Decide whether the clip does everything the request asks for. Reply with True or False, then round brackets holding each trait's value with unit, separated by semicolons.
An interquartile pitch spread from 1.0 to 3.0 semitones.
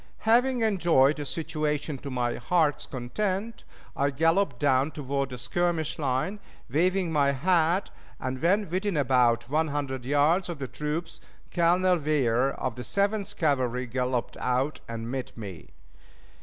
False (5.2 semitones)